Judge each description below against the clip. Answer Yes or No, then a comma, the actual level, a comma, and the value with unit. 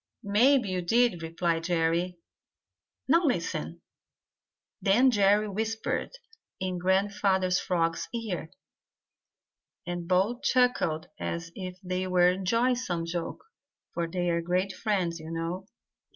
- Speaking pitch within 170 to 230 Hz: Yes, medium, 185 Hz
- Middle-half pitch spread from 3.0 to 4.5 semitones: Yes, average, 3.6 semitones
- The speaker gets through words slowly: Yes, slow, 115 wpm